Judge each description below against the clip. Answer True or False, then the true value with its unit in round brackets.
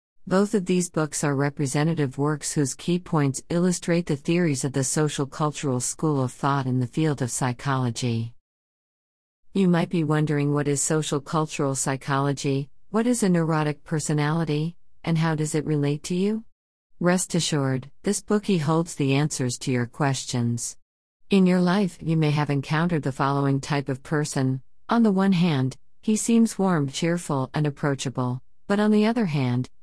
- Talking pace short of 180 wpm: True (165 wpm)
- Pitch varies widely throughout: False (4.0 semitones)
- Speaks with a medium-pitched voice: True (150 Hz)